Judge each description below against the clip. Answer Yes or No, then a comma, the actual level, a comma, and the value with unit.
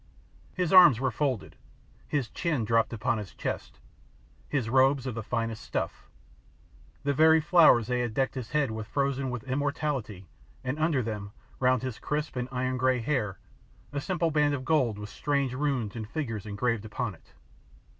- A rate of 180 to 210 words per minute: No, average, 170 wpm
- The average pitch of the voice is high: No, low, 130 Hz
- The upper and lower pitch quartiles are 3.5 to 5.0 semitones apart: Yes, average, 4.2 semitones